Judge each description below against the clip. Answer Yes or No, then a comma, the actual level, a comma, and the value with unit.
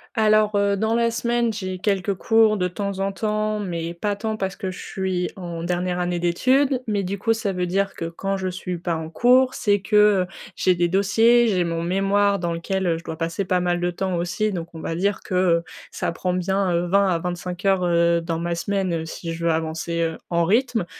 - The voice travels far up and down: No, average, 2.9 semitones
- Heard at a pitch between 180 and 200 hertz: Yes, medium, 185 Hz